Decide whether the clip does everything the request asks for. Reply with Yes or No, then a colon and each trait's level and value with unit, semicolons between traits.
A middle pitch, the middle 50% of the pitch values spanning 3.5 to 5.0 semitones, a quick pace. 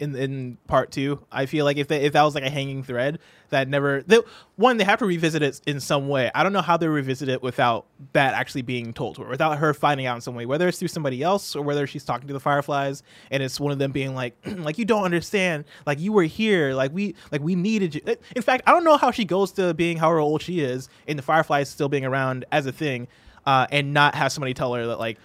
Yes: medium, 145 Hz; average, 4.0 semitones; fast, 270 wpm